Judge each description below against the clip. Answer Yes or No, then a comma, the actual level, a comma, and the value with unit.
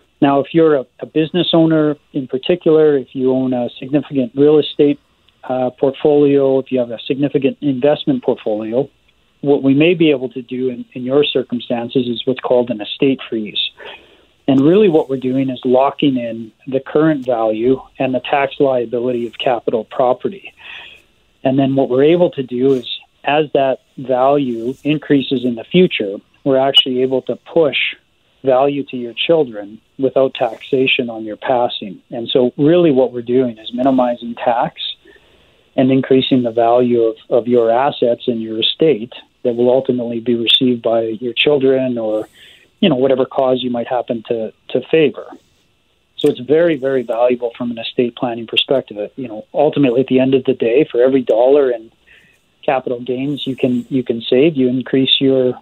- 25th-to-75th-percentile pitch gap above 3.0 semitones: No, narrow, 2.4 semitones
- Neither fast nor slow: Yes, average, 175 wpm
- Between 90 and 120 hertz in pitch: No, low, 130 Hz